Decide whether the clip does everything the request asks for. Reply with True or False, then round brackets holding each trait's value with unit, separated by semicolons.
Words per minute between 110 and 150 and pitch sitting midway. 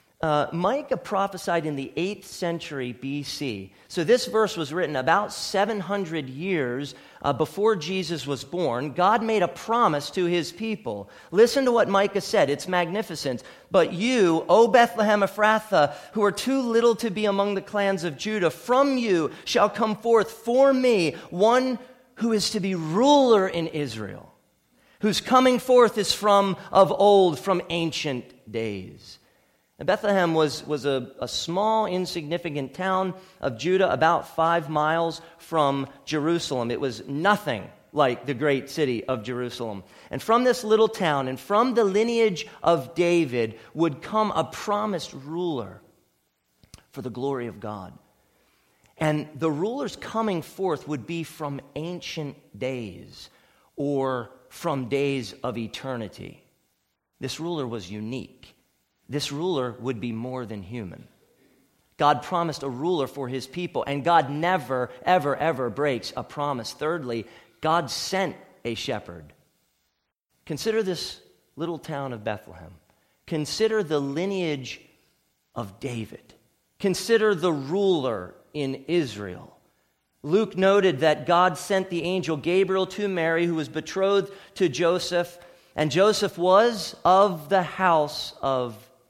True (140 wpm; 165 Hz)